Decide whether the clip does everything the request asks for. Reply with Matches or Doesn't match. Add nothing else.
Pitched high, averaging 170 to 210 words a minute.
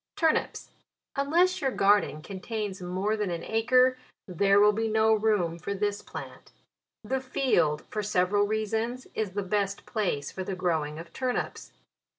Doesn't match